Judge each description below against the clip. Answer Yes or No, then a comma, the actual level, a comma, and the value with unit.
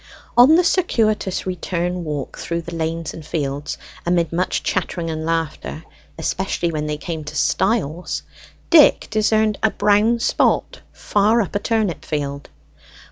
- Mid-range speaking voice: Yes, medium, 175 Hz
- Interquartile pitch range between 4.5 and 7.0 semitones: Yes, average, 5.1 semitones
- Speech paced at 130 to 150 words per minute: Yes, average, 140 wpm